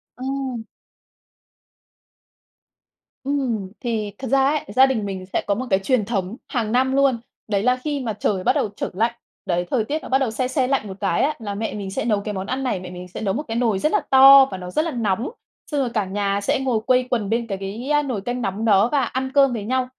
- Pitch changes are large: No, average, 4.7 semitones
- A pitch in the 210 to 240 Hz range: Yes, high, 230 Hz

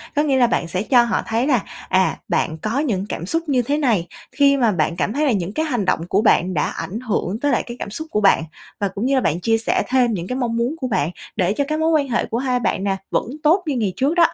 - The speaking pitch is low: No, high, 235 Hz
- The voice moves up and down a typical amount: No, wide, 6.0 semitones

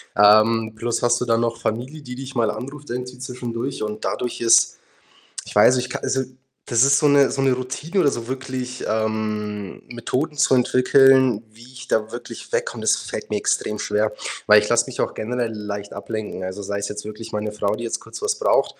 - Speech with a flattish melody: No, average, 3.1 semitones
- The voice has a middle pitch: No, low, 120 Hz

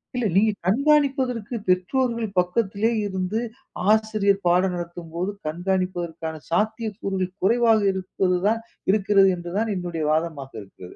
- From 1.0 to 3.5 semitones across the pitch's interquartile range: No, average, 3.9 semitones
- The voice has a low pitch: No, high, 190 Hz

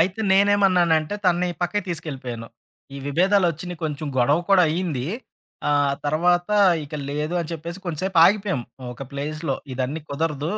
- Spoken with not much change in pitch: No, average, 3.9 semitones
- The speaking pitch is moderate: Yes, medium, 165 Hz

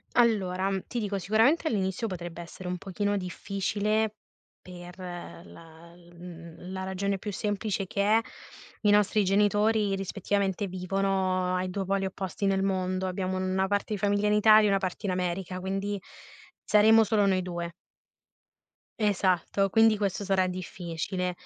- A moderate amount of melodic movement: No, narrow, 2.0 semitones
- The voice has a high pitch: Yes, high, 195 Hz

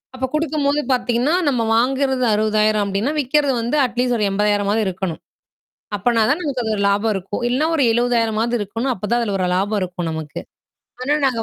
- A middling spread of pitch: Yes, average, 4.1 semitones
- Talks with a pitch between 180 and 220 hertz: No, high, 230 Hz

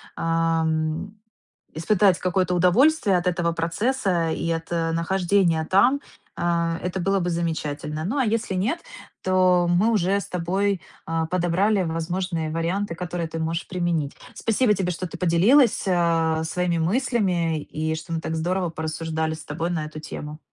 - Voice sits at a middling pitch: Yes, medium, 175 Hz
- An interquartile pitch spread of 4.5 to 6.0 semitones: No, average, 2.7 semitones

